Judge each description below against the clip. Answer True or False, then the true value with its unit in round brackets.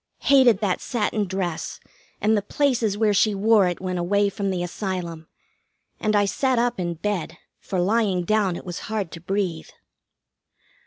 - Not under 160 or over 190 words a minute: True (165 wpm)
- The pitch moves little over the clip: False (3.2 semitones)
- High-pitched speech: True (200 Hz)